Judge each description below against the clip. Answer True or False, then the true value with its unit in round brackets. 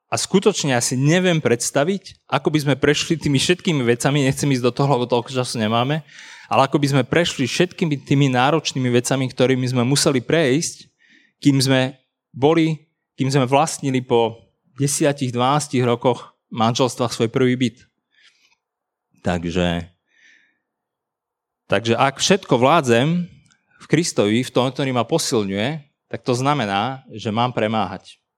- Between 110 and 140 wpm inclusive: True (135 wpm)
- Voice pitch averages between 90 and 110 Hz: False (135 Hz)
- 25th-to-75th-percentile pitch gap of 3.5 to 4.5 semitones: True (3.8 semitones)